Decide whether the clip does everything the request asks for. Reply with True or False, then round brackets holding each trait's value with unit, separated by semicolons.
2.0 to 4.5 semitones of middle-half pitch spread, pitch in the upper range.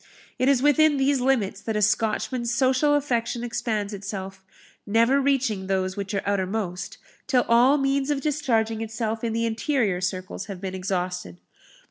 False (5.4 semitones; 225 Hz)